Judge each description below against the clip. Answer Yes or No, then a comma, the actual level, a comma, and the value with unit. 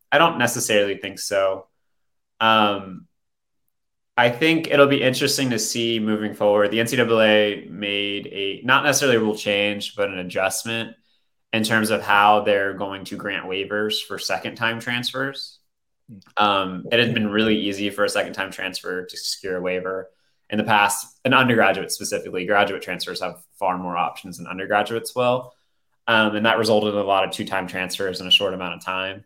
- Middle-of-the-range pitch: No, low, 105 Hz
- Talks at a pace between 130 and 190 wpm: Yes, average, 180 wpm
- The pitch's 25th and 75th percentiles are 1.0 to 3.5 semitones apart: Yes, average, 2.8 semitones